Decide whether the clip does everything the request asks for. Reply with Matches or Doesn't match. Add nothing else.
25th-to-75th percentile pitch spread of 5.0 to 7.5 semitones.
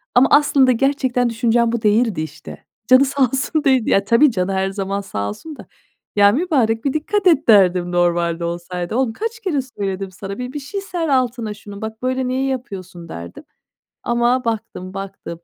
Matches